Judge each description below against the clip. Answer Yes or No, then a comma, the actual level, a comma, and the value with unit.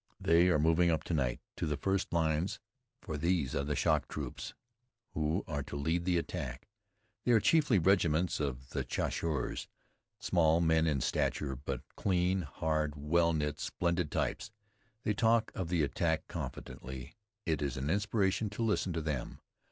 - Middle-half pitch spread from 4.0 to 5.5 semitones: No, average, 3.3 semitones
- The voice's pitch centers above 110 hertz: No, very low, 80 Hz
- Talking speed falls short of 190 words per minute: Yes, average, 160 wpm